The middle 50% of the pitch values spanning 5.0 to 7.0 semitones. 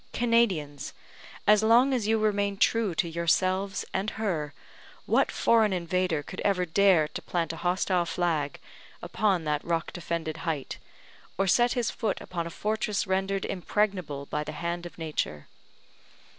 No: average, 4.0 semitones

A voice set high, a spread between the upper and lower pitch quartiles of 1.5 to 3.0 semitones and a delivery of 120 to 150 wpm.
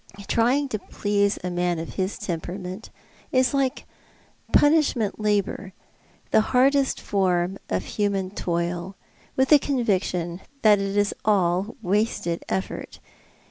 No: high, 200 Hz; average, 4.1 semitones; average, 140 wpm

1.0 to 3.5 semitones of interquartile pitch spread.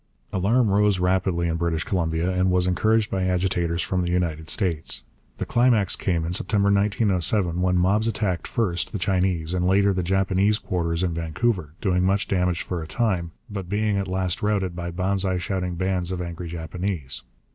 Yes: narrow, 2.4 semitones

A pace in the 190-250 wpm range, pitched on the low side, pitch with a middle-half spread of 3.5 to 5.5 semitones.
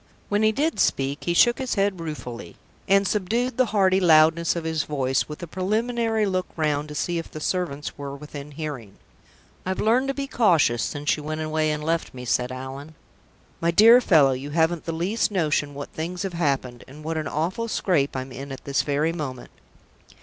No: average, 200 wpm; medium, 160 Hz; average, 4.9 semitones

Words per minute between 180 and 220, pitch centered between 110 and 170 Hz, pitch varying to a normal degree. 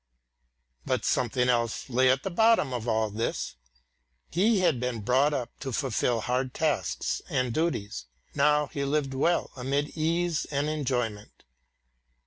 No: average, 140 wpm; low, 135 Hz; average, 3.8 semitones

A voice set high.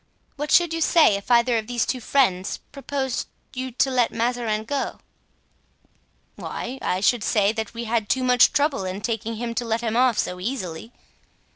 Yes: high, 235 Hz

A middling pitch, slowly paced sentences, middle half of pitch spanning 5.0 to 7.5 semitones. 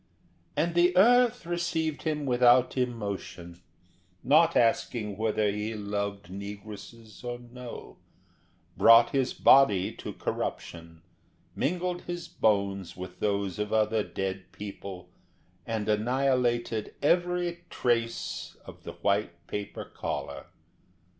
No: low, 115 Hz; slow, 110 wpm; wide, 5.5 semitones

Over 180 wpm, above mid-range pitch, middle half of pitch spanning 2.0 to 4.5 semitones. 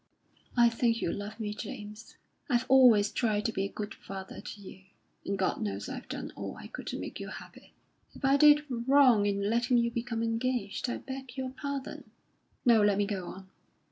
Yes: average, 200 wpm; high, 230 Hz; average, 3.7 semitones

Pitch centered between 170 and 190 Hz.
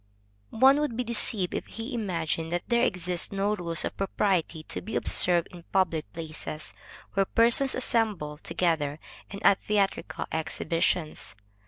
Yes: medium, 185 Hz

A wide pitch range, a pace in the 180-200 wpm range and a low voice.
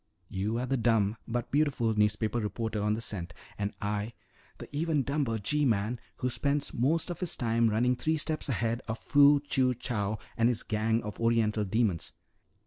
No: average, 3.9 semitones; average, 185 wpm; low, 115 Hz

